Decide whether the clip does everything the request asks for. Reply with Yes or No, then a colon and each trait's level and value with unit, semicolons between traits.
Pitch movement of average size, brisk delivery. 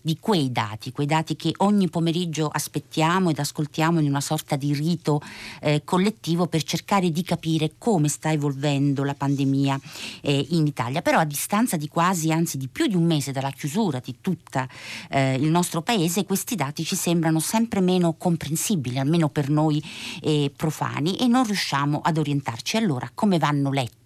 Yes: average, 3.4 semitones; fast, 175 wpm